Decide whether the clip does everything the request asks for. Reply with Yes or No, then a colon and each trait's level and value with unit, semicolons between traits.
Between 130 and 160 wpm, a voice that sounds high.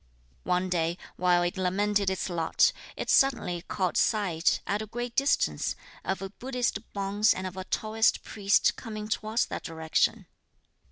Yes: average, 155 wpm; high, 195 Hz